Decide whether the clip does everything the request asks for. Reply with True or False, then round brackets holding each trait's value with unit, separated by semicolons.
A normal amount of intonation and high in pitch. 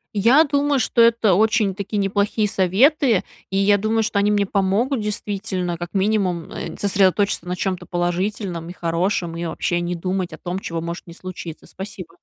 True (3.2 semitones; 195 Hz)